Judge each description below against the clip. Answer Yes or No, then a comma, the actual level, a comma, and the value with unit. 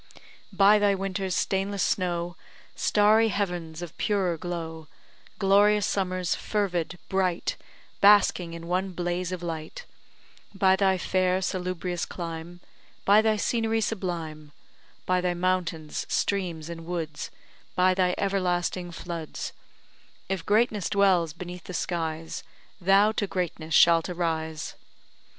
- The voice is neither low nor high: Yes, medium, 180 Hz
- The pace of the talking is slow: Yes, slow, 120 wpm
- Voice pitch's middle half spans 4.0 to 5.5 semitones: No, narrow, 2.5 semitones